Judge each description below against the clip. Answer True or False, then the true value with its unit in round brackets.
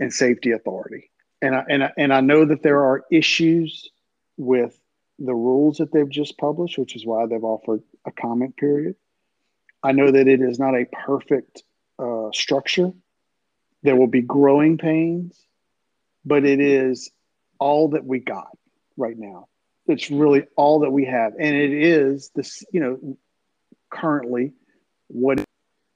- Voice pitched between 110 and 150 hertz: True (140 Hz)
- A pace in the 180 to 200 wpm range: False (155 wpm)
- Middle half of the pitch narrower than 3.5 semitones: True (2.7 semitones)